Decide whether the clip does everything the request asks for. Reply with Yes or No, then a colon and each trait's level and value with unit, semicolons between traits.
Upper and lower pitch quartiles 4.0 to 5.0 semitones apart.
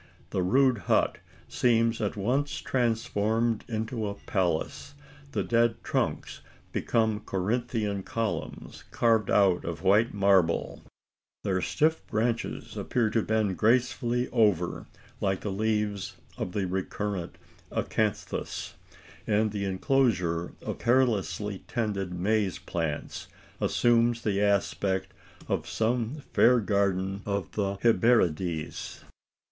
No: average, 3.3 semitones